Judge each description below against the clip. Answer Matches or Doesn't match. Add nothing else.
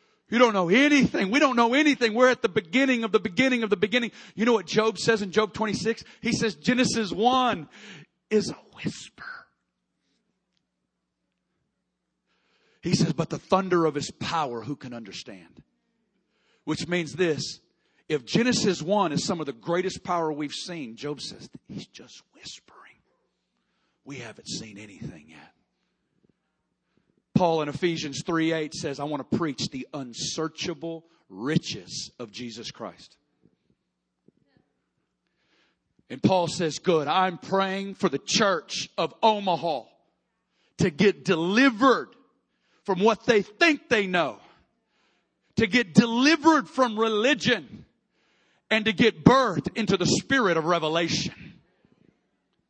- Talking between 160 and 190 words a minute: Doesn't match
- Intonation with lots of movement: Matches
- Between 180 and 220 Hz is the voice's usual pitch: Matches